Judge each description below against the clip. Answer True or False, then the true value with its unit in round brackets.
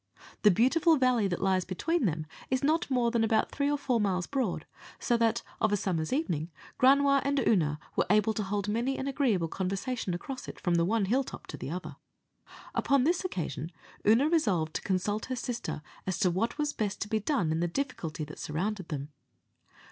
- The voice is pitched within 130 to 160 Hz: False (215 Hz)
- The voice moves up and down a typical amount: False (6.6 semitones)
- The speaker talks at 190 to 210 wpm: True (200 wpm)